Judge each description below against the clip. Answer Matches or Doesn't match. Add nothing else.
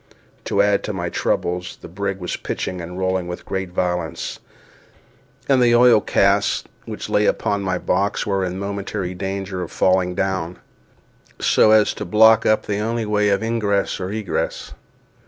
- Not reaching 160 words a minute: Doesn't match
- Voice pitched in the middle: Doesn't match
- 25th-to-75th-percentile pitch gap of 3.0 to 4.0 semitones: Doesn't match